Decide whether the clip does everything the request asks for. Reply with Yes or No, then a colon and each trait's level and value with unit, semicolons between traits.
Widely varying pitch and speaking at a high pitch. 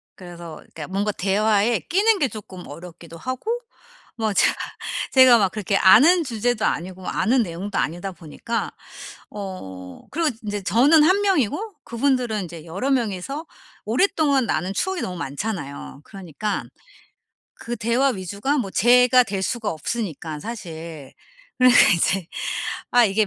Yes: wide, 5.9 semitones; high, 210 Hz